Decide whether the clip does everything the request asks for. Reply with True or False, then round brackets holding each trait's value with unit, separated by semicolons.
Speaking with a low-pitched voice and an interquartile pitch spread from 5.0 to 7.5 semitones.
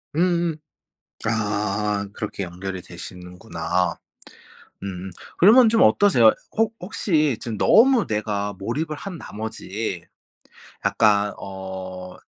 False (105 Hz; 8.5 semitones)